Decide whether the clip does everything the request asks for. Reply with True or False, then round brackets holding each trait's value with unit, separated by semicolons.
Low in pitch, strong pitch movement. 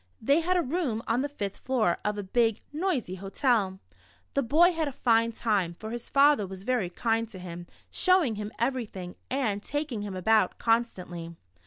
False (225 Hz; 5.7 semitones)